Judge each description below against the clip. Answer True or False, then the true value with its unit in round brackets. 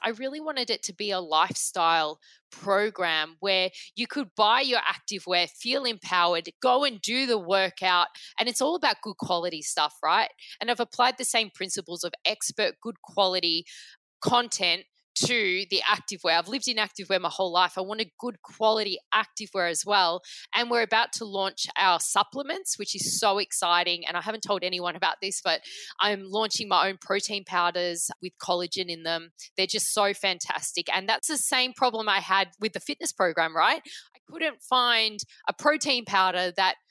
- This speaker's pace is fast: False (185 wpm)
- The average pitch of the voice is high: True (200 Hz)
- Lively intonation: False (4.7 semitones)